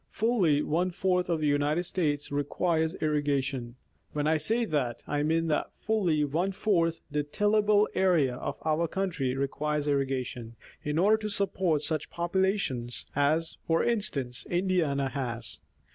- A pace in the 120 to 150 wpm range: Yes, average, 145 wpm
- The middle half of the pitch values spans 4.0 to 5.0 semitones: Yes, average, 4.4 semitones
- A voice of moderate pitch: Yes, medium, 155 Hz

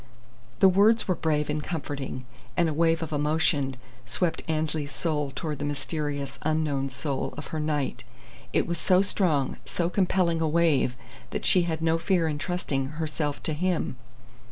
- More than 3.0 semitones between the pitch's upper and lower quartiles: No, narrow, 2.6 semitones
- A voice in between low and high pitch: Yes, medium, 155 Hz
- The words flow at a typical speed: Yes, average, 165 wpm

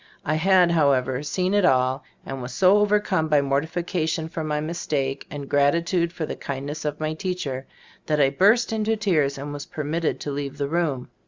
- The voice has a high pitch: No, medium, 155 Hz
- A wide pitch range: No, average, 3.8 semitones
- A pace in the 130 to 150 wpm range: No, average, 200 wpm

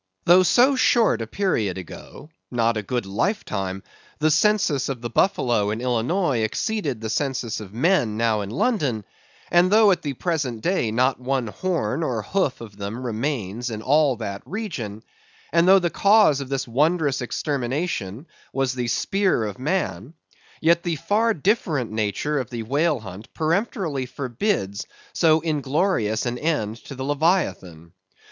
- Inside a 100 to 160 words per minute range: Yes, average, 155 wpm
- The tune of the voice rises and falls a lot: Yes, wide, 7.3 semitones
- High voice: No, low, 135 Hz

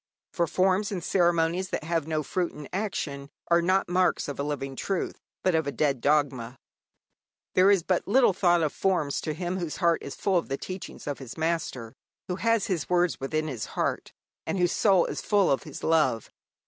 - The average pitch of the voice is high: No, medium, 170 Hz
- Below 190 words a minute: No, average, 200 wpm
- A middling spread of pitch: Yes, average, 4.1 semitones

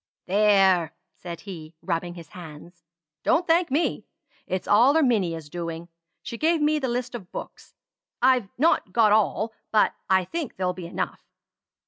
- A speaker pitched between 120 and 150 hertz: No, high, 200 Hz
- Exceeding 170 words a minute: No, average, 150 wpm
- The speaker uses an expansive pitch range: Yes, wide, 6.6 semitones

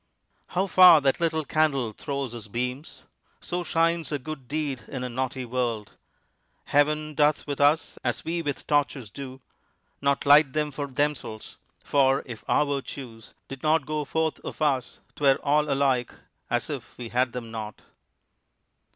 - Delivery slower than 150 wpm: No, average, 160 wpm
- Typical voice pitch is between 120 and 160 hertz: Yes, medium, 140 Hz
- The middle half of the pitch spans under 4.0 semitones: Yes, average, 3.1 semitones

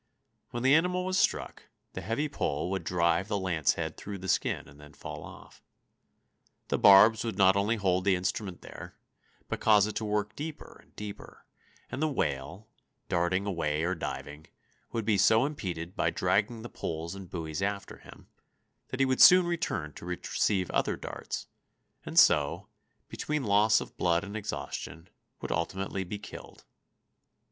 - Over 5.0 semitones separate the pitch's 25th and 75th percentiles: No, average, 4.3 semitones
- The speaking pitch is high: No, low, 100 Hz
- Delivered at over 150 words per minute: Yes, average, 165 wpm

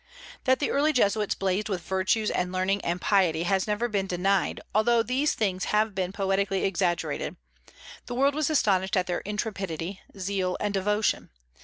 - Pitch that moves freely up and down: No, narrow, 2.5 semitones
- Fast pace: No, average, 165 wpm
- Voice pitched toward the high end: Yes, high, 195 Hz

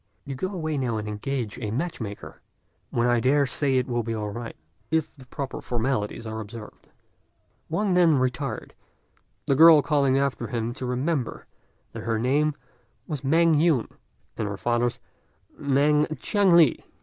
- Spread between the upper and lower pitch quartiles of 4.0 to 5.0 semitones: Yes, average, 4.3 semitones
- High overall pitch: No, low, 130 Hz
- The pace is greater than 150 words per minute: Yes, average, 160 wpm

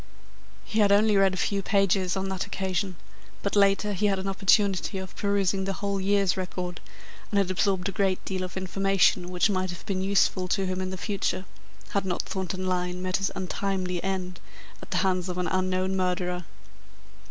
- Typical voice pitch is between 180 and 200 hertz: Yes, high, 190 Hz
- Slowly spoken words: No, average, 190 wpm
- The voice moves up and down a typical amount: No, narrow, 1.3 semitones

